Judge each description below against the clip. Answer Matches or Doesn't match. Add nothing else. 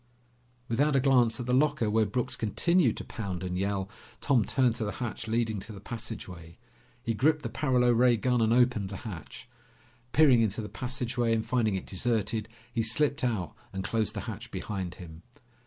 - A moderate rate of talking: Matches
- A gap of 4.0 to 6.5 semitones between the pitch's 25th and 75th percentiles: Doesn't match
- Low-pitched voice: Matches